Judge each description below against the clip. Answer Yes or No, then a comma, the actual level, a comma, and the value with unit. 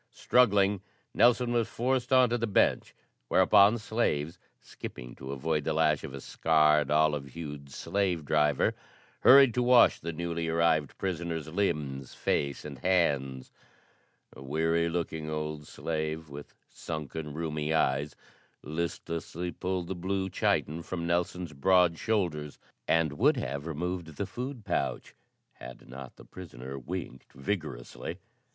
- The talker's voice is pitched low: Yes, very low, 80 Hz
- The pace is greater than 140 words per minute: No, slow, 135 wpm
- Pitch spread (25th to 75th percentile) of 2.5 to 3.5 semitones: No, average, 3.9 semitones